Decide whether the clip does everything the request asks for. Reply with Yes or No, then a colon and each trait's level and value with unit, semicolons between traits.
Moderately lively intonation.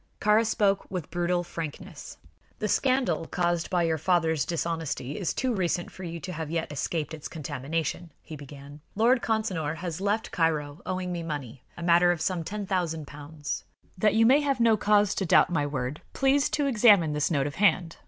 Yes: average, 4.6 semitones